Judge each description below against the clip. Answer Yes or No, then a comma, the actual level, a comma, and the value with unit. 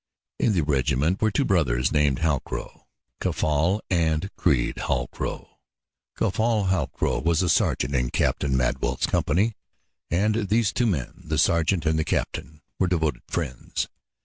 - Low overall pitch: Yes, very low, 80 Hz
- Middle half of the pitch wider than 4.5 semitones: Yes, average, 5.1 semitones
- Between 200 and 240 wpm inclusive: No, average, 140 wpm